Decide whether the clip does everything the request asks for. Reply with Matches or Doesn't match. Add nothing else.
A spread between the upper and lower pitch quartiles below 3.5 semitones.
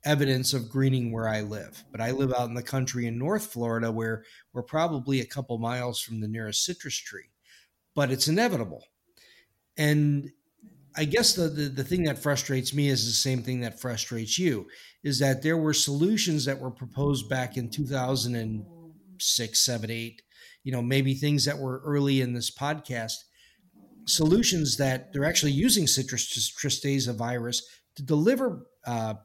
Doesn't match